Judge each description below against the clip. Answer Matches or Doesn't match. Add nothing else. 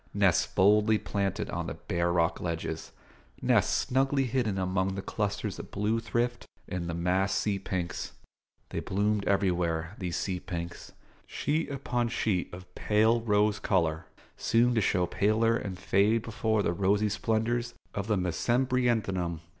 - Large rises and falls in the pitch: Doesn't match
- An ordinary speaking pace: Matches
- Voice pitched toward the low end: Matches